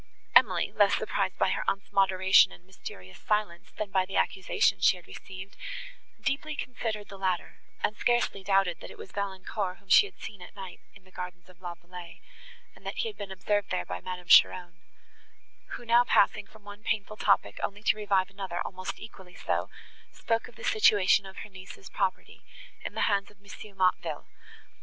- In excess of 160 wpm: Yes, average, 190 wpm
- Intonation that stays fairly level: Yes, narrow, 2.2 semitones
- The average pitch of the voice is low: No, high, 195 Hz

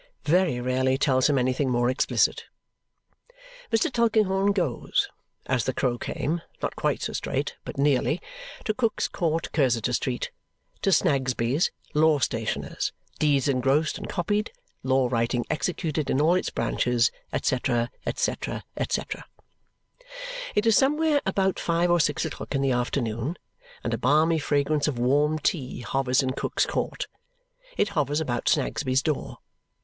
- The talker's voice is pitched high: No, medium, 145 Hz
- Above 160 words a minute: No, average, 140 wpm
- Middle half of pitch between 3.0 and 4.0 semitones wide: No, average, 5.0 semitones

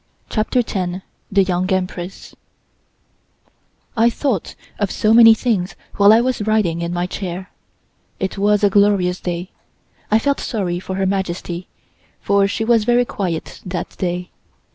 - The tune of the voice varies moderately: Yes, average, 3.3 semitones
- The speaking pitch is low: No, high, 195 Hz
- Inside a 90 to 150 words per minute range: Yes, average, 145 wpm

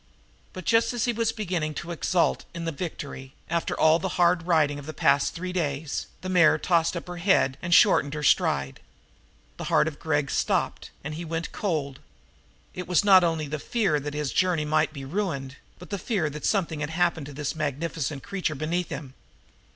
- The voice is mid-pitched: Yes, medium, 160 Hz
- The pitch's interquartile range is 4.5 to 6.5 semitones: No, average, 3.4 semitones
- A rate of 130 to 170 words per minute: No, average, 195 wpm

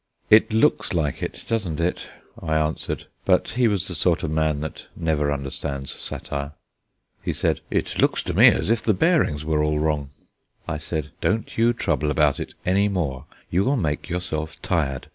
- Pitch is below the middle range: Yes, very low, 80 Hz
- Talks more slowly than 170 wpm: No, average, 180 wpm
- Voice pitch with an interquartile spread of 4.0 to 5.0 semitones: Yes, average, 4.4 semitones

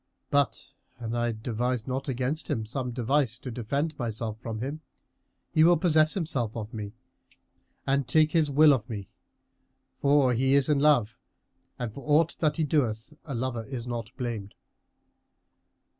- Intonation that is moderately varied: Yes, average, 4.3 semitones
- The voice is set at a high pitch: No, low, 130 Hz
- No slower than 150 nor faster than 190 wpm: Yes, average, 160 wpm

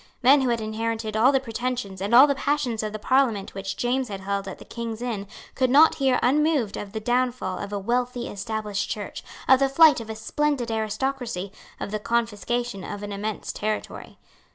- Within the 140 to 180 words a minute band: No, average, 200 wpm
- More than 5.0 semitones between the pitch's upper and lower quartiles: No, average, 3.6 semitones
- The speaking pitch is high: Yes, high, 230 Hz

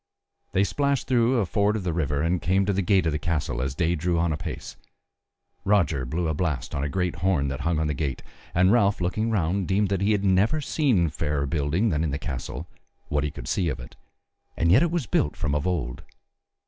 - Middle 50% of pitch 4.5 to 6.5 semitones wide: Yes, average, 5.2 semitones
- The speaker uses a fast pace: Yes, fast, 225 wpm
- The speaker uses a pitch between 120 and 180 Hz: No, very low, 85 Hz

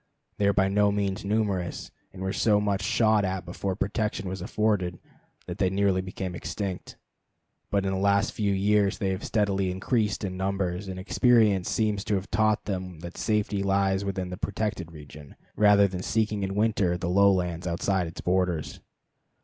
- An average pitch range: No, narrow, 1.9 semitones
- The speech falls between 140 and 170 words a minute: No, average, 180 wpm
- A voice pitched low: Yes, very low, 95 Hz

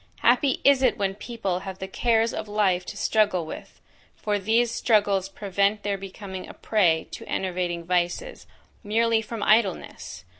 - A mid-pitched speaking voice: No, high, 205 Hz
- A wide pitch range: No, average, 3.1 semitones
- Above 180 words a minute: No, average, 155 wpm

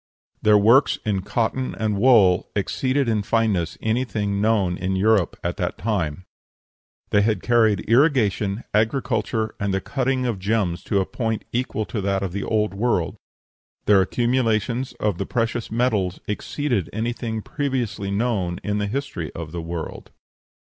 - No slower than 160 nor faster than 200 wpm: No, average, 150 wpm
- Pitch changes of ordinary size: Yes, average, 3.4 semitones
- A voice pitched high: No, low, 110 Hz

